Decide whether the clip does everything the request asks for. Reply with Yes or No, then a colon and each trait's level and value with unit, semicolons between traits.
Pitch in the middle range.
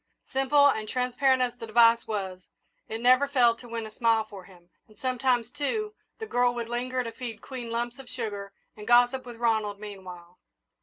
No: high, 235 Hz